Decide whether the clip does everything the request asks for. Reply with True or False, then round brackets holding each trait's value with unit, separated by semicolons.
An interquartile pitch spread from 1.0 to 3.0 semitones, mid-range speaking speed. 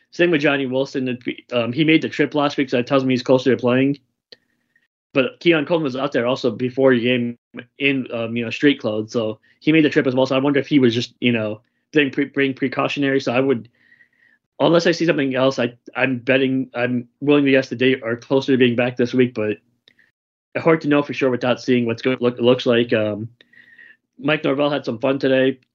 False (2.6 semitones; 235 wpm)